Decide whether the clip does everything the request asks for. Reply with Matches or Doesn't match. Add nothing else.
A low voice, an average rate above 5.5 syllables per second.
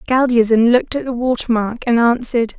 Doesn't match